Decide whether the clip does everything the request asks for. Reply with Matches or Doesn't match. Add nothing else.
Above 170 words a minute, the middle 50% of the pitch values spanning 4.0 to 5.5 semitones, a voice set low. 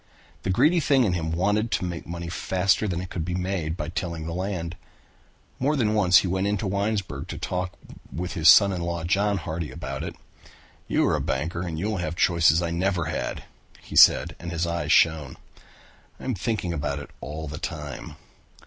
Doesn't match